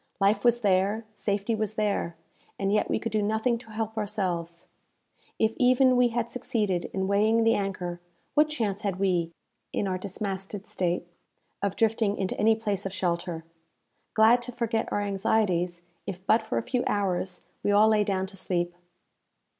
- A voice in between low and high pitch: No, high, 205 Hz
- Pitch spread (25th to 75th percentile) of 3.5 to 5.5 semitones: No, average, 2.9 semitones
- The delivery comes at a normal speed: Yes, average, 170 wpm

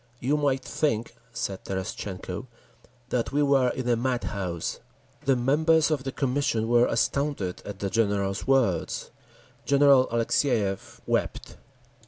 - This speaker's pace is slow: Yes, slow, 125 wpm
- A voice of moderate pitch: No, low, 125 Hz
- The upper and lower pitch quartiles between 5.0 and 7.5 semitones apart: Yes, average, 5.3 semitones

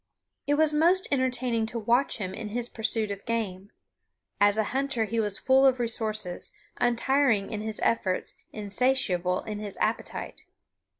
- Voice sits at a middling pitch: No, high, 225 Hz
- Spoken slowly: No, average, 155 wpm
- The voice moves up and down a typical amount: Yes, average, 3.8 semitones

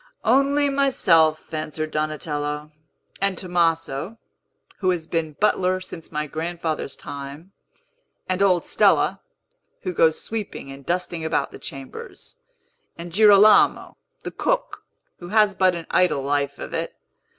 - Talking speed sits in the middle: No, slow, 130 wpm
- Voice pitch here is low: No, medium, 170 Hz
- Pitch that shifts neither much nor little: Yes, average, 3.9 semitones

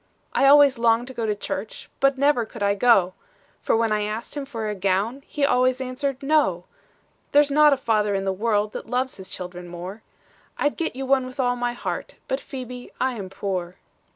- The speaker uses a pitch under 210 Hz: No, high, 235 Hz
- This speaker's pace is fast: Yes, fast, 210 wpm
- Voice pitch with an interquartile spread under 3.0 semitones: No, average, 4.8 semitones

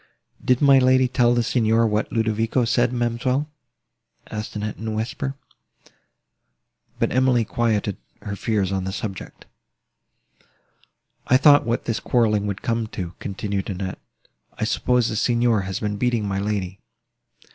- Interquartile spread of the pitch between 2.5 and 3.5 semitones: Yes, average, 3.0 semitones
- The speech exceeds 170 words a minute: No, average, 145 wpm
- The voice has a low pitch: Yes, low, 115 Hz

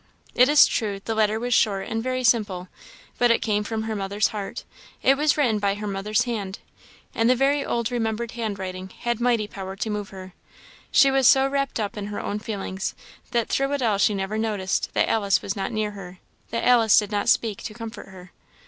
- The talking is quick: Yes, fast, 215 wpm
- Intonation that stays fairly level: No, average, 3.0 semitones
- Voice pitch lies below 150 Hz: No, high, 215 Hz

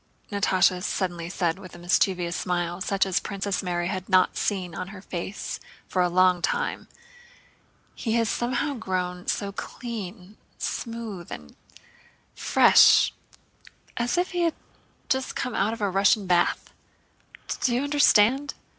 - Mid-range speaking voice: No, high, 195 Hz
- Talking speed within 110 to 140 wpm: Yes, slow, 135 wpm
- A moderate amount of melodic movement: Yes, average, 4.2 semitones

